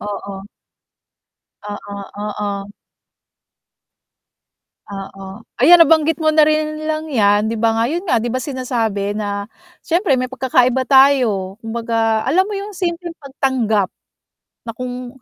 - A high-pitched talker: Yes, very high, 250 Hz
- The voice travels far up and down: Yes, wide, 6.5 semitones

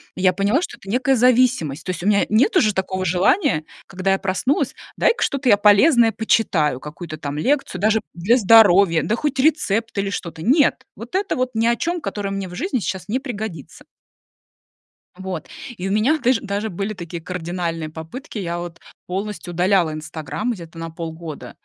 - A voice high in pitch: Yes, high, 195 Hz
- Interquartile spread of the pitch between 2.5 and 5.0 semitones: No, wide, 5.5 semitones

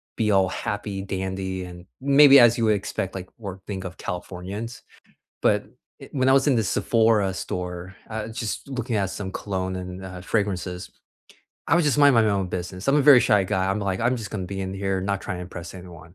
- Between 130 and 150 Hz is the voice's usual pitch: No, very low, 95 Hz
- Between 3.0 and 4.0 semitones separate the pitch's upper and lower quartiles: Yes, average, 3.6 semitones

